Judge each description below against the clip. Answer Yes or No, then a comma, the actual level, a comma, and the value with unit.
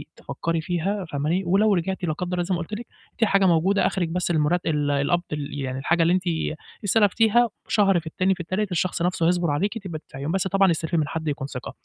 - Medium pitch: Yes, medium, 175 Hz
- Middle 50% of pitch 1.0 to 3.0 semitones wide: No, average, 3.4 semitones